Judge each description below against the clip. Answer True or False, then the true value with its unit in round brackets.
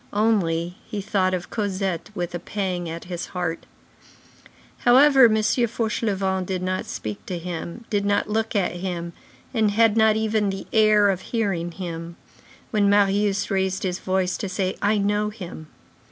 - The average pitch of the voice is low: False (195 Hz)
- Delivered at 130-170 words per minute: True (160 wpm)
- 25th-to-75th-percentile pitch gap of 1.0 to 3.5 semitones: True (3.0 semitones)